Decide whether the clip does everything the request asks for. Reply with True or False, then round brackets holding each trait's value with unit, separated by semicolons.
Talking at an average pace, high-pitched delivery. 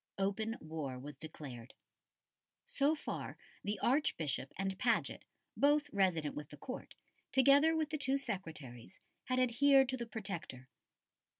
False (130 wpm; 200 Hz)